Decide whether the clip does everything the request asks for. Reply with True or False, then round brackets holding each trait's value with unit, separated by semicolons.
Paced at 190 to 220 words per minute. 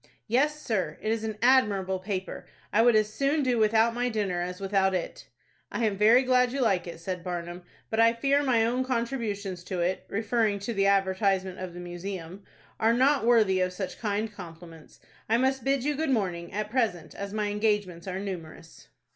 True (195 wpm)